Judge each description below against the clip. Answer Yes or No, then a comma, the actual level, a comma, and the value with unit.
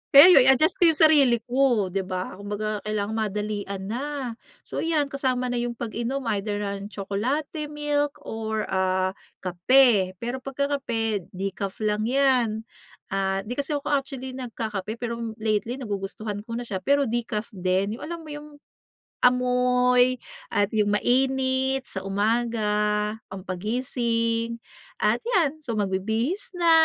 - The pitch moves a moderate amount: Yes, average, 4.4 semitones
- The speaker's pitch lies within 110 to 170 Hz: No, high, 235 Hz